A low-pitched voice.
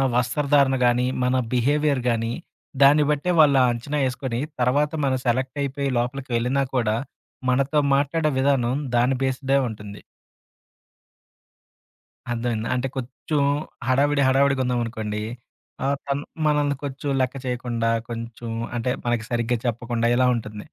Yes: low, 130 Hz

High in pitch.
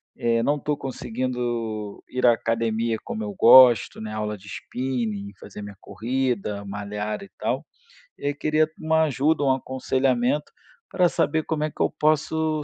No: low, 125 Hz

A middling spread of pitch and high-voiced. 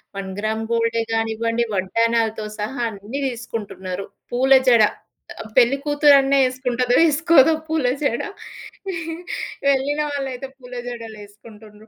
Yes: average, 3.4 semitones; high, 235 Hz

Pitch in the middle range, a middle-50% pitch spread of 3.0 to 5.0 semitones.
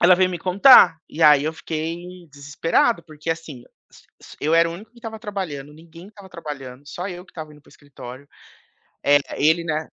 Yes: medium, 165 Hz; average, 3.5 semitones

